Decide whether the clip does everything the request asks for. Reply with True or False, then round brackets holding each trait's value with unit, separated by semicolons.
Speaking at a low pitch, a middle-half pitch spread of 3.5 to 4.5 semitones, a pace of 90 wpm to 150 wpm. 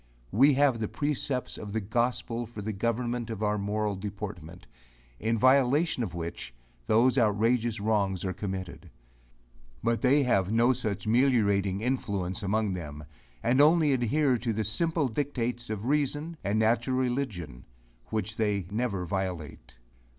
True (110 Hz; 4.0 semitones; 145 wpm)